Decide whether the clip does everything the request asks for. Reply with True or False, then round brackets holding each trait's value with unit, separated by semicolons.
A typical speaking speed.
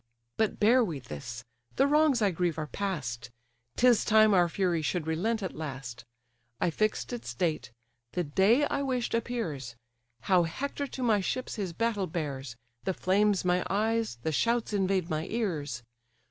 True (160 wpm)